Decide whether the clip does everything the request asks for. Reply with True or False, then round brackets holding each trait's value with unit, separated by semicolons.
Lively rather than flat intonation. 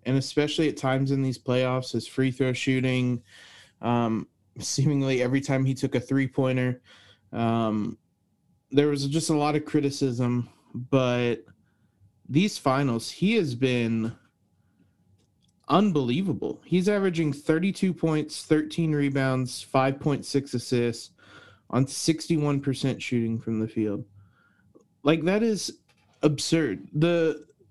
False (4.2 semitones)